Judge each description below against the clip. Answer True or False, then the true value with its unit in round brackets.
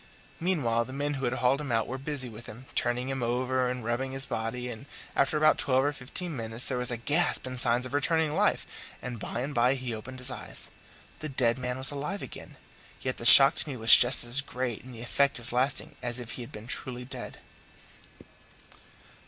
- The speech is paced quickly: True (220 wpm)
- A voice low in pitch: True (130 Hz)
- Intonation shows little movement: True (2.3 semitones)